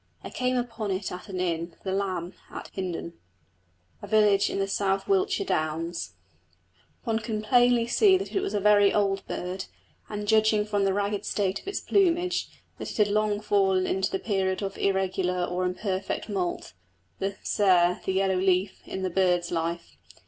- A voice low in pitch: No, high, 195 Hz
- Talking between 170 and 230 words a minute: Yes, average, 180 wpm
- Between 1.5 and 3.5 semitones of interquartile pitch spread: Yes, narrow, 2.5 semitones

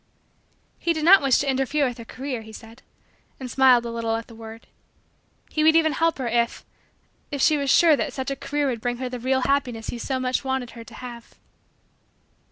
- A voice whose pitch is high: Yes, very high, 260 Hz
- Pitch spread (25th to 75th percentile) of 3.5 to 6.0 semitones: No, average, 3.1 semitones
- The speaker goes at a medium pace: No, fast, 215 wpm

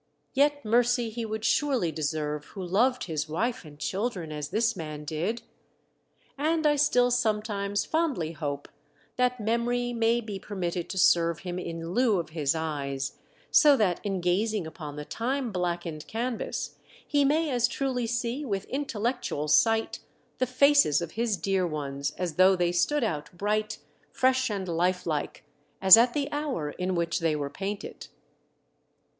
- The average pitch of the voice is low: No, high, 200 Hz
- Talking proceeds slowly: No, average, 160 wpm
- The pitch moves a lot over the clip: Yes, wide, 6.6 semitones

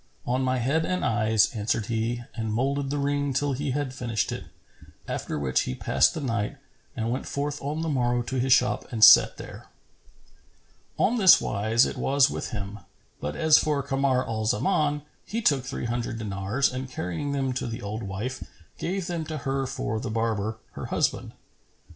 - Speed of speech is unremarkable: Yes, average, 185 wpm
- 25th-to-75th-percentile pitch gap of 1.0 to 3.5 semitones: No, average, 4.1 semitones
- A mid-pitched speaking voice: No, low, 130 Hz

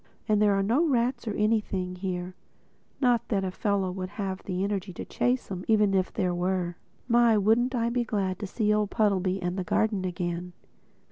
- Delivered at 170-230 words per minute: Yes, average, 190 wpm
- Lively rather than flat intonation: No, average, 3.1 semitones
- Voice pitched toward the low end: No, high, 200 Hz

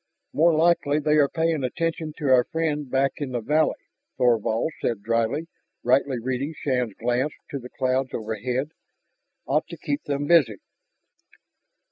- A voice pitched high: No, low, 135 Hz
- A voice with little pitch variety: No, average, 3.7 semitones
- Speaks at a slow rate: No, average, 145 wpm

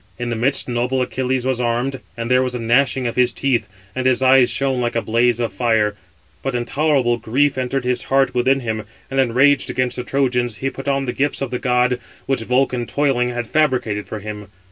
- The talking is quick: Yes, fast, 210 wpm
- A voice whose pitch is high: No, low, 125 Hz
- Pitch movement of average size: No, narrow, 2.0 semitones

